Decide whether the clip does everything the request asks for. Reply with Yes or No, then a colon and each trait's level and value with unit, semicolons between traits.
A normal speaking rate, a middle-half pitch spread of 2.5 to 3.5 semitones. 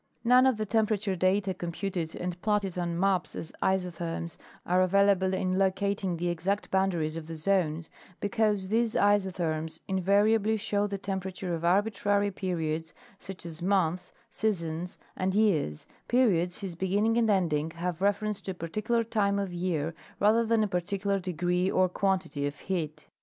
Yes: average, 150 wpm; average, 2.9 semitones